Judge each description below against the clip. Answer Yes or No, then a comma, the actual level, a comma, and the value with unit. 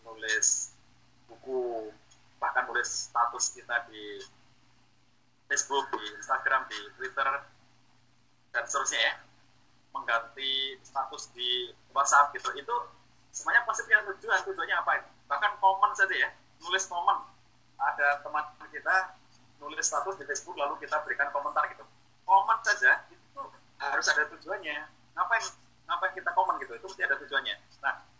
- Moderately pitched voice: Yes, medium, 180 Hz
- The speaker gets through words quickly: No, average, 130 wpm